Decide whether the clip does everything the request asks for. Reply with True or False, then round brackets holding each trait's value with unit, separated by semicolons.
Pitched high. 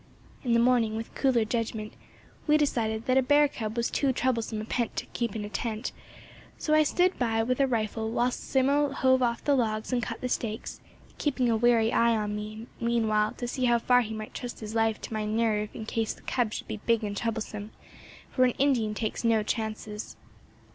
True (230 Hz)